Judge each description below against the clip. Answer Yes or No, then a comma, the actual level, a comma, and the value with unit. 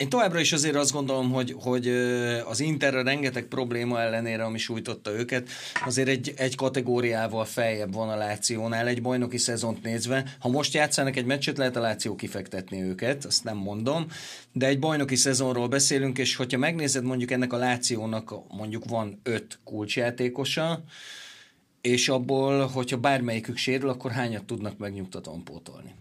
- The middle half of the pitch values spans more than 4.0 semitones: No, average, 2.8 semitones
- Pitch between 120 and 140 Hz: Yes, low, 125 Hz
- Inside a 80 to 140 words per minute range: No, fast, 155 wpm